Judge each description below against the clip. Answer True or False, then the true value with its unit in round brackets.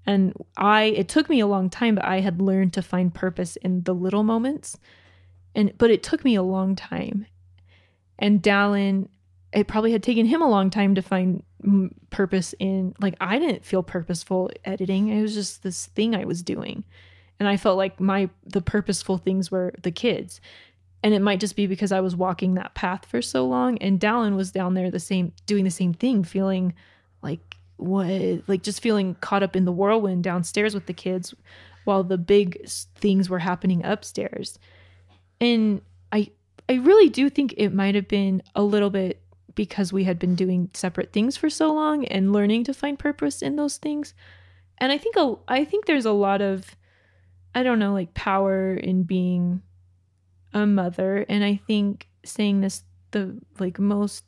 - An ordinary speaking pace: True (190 wpm)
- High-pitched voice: True (195 Hz)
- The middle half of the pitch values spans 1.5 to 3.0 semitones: True (2.5 semitones)